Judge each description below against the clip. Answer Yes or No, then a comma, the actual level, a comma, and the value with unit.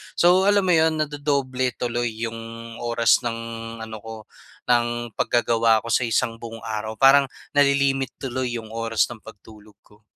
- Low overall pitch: Yes, low, 120 Hz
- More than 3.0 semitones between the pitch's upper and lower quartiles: Yes, average, 3.4 semitones